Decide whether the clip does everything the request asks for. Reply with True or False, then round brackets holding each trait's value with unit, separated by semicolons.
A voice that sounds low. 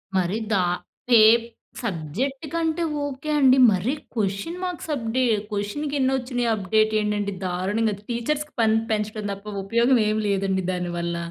False (220 Hz)